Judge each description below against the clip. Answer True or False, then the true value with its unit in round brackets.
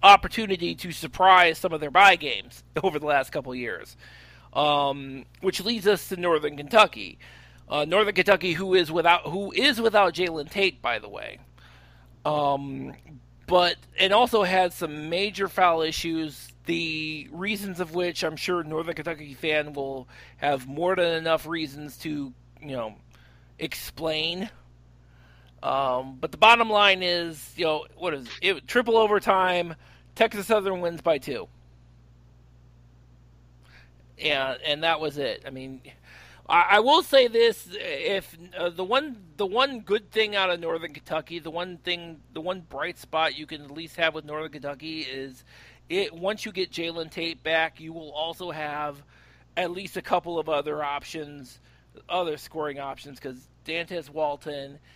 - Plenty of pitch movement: False (4.8 semitones)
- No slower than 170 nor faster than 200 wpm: False (160 wpm)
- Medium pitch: True (160 Hz)